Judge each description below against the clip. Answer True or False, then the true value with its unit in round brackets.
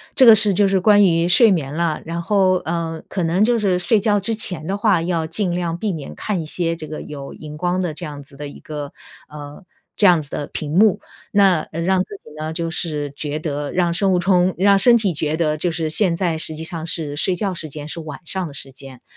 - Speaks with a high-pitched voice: False (170 Hz)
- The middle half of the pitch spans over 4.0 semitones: False (3.7 semitones)